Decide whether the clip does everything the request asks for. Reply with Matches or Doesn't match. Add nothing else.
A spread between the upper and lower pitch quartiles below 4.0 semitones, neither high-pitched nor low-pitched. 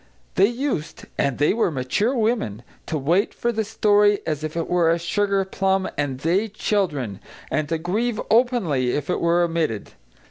Doesn't match